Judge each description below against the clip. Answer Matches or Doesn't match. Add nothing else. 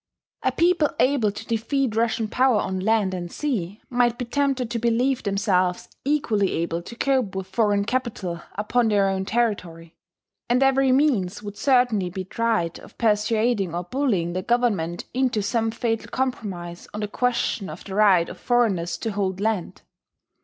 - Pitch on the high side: Matches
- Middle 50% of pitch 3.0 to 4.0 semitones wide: Doesn't match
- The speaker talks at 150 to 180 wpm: Matches